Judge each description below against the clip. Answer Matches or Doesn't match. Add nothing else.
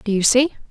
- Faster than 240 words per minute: Matches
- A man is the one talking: Doesn't match